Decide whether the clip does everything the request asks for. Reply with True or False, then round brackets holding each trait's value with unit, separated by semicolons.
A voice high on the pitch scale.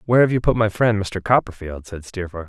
False (100 Hz)